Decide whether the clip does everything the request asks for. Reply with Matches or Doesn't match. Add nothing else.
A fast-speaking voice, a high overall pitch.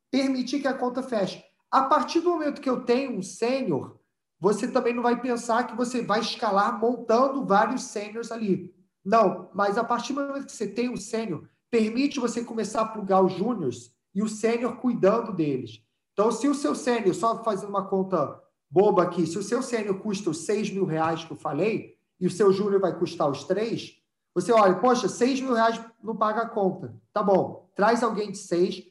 Matches